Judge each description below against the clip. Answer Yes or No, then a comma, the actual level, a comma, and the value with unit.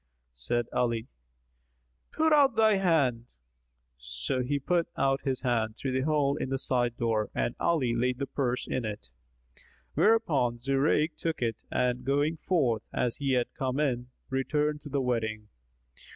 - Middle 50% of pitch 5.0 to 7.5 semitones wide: No, average, 3.8 semitones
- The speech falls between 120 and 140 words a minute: No, average, 155 wpm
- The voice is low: Yes, low, 130 Hz